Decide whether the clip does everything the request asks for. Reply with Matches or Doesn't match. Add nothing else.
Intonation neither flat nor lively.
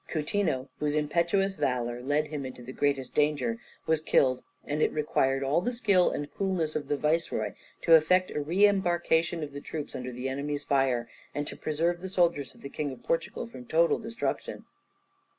Matches